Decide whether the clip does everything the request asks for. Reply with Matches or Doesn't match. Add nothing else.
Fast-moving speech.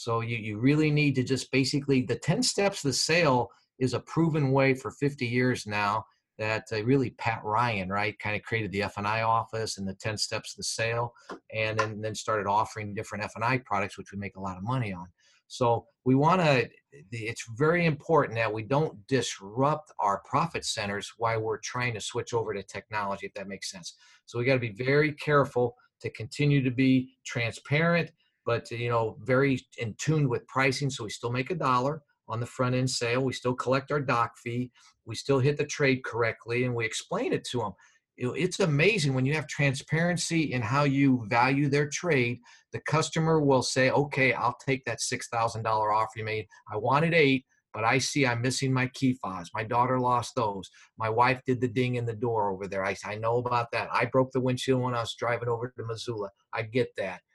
Matches